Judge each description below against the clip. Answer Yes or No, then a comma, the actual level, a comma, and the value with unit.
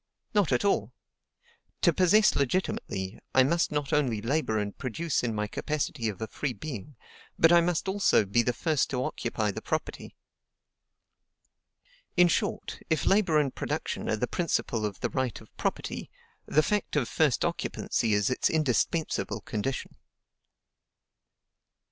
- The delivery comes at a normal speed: Yes, average, 150 wpm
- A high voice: No, medium, 140 Hz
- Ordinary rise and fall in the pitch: No, wide, 6.2 semitones